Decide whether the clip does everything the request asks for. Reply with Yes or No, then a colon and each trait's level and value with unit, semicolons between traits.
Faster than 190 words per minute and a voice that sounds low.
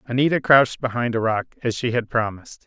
Yes: fast, 205 wpm; low, 120 Hz